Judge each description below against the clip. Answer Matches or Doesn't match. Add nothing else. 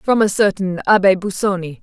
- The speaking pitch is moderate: Doesn't match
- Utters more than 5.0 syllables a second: Matches